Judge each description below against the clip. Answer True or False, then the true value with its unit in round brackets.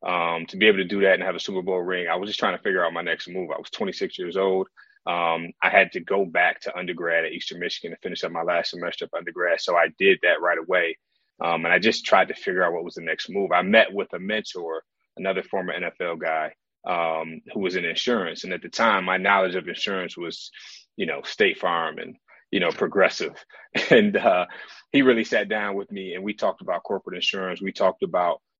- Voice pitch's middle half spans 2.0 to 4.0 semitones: True (2.9 semitones)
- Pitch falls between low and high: False (95 Hz)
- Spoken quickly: True (240 wpm)